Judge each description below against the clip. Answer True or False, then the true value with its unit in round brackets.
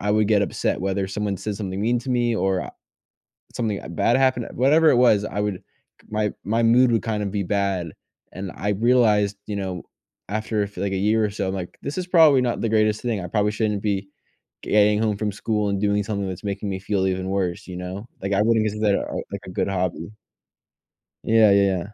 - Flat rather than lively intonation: True (2.3 semitones)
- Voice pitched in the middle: False (105 Hz)